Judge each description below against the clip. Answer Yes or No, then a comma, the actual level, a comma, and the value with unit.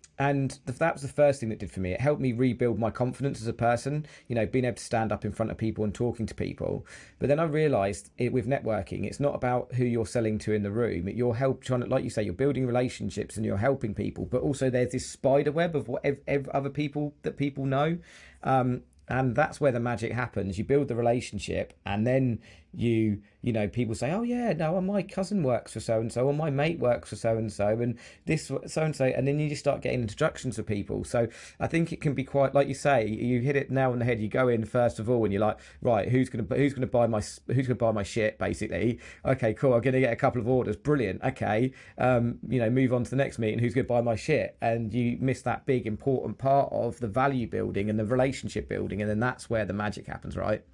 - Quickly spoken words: Yes, fast, 255 wpm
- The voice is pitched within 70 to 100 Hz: No, low, 125 Hz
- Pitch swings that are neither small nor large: Yes, average, 3.6 semitones